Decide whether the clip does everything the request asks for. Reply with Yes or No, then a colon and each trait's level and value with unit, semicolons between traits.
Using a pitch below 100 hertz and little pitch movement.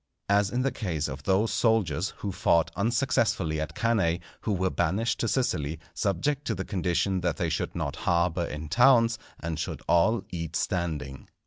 No: very low, 90 Hz; average, 5.3 semitones